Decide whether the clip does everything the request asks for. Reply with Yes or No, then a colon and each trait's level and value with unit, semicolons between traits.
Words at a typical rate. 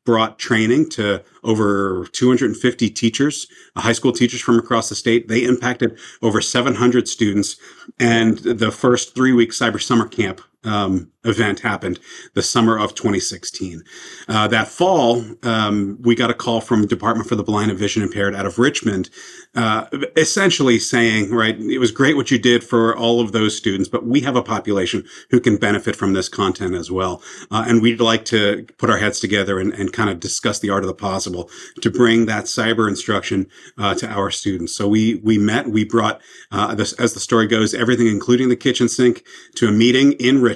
Yes: average, 190 wpm